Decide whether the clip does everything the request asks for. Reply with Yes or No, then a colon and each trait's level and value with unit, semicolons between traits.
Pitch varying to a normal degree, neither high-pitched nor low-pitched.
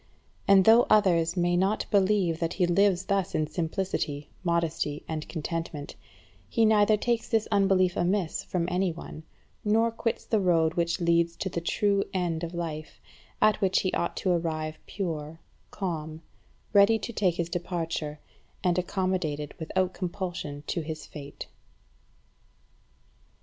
Yes: average, 3.2 semitones; medium, 175 Hz